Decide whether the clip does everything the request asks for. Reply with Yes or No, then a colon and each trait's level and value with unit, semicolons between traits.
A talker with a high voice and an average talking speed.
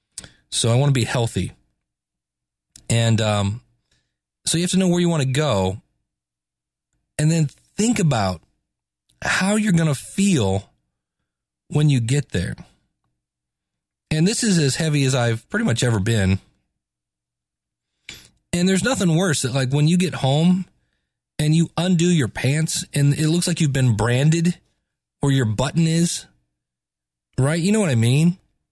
No: low, 135 Hz; average, 155 wpm